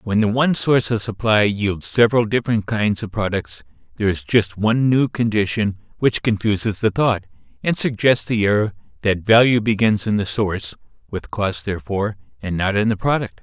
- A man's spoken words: Yes, male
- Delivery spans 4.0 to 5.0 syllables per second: No, 5.2 syllables/s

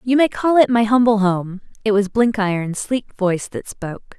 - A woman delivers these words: Yes, female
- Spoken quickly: No, average, 185 wpm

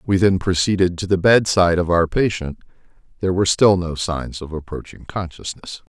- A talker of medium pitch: No, very low, 90 Hz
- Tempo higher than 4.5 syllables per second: Yes, 5.5 syllables/s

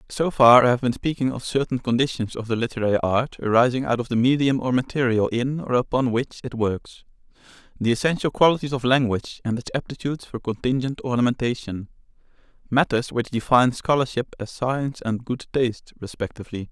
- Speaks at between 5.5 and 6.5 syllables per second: Yes, 5.9 syllables/s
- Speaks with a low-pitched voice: Yes, low, 125 Hz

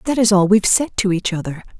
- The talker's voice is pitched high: Yes, high, 200 Hz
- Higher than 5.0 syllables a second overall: Yes, 6.6 syllables/s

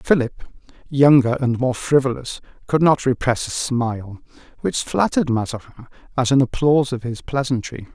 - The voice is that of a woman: No, male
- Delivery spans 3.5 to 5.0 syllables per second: No, 5.4 syllables/s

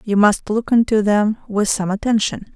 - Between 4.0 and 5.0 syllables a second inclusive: Yes, 4.7 syllables/s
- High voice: Yes, high, 210 Hz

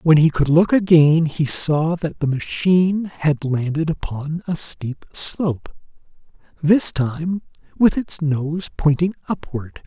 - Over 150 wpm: No, average, 140 wpm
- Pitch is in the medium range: Yes, medium, 160 Hz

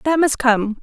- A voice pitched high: Yes, very high, 260 Hz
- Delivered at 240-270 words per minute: No, fast, 215 wpm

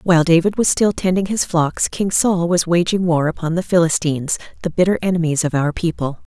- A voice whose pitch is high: No, medium, 170 Hz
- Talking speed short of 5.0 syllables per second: No, 5.6 syllables/s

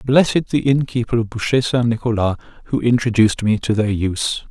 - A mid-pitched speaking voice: No, low, 115 Hz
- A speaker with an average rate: Yes, average, 175 wpm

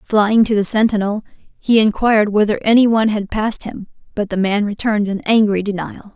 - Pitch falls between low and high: No, high, 210 Hz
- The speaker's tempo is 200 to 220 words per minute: No, average, 185 wpm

